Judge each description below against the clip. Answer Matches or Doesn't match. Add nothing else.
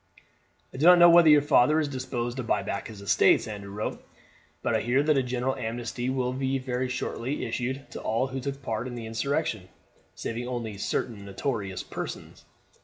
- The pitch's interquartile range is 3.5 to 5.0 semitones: Doesn't match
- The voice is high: Doesn't match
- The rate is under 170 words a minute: Doesn't match